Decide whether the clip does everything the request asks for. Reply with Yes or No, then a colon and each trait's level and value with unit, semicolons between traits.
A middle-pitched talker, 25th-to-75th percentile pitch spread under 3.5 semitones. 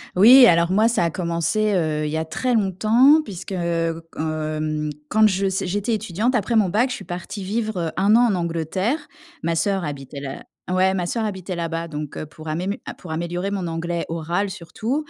No: medium, 180 Hz; average, 4.4 semitones